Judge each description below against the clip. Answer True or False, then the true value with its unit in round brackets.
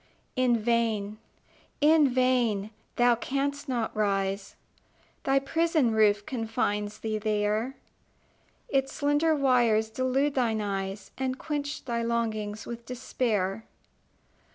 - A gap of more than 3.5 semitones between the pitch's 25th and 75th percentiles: True (3.9 semitones)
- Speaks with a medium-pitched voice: False (235 Hz)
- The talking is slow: True (105 wpm)